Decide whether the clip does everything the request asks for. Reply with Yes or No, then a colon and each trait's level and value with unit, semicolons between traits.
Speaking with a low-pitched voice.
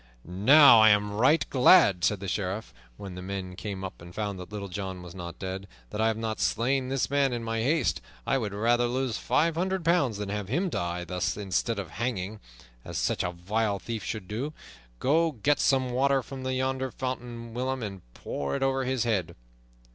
Yes: low, 110 Hz